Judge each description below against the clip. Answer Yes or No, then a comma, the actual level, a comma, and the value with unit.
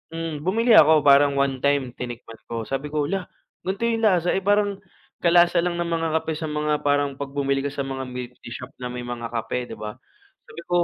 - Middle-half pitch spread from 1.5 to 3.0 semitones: No, average, 4.5 semitones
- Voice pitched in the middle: Yes, medium, 145 Hz